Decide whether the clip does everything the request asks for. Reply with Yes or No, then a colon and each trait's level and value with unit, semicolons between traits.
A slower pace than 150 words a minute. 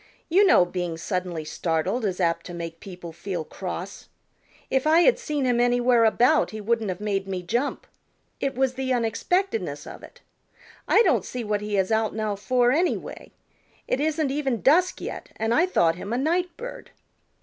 No: average, 185 wpm